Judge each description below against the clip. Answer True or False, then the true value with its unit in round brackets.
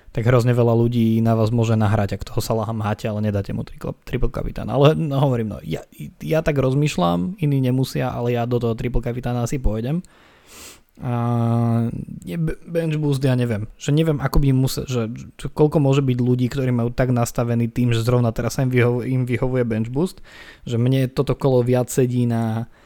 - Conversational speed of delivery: False (190 wpm)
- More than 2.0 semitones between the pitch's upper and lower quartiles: True (2.7 semitones)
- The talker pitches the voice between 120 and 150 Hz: True (125 Hz)